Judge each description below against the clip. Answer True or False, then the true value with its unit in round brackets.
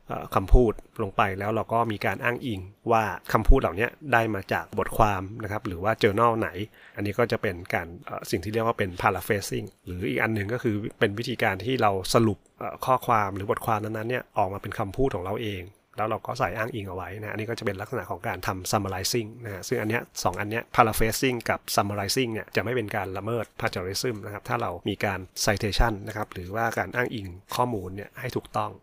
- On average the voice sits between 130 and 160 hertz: False (110 Hz)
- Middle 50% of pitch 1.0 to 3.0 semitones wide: True (2.5 semitones)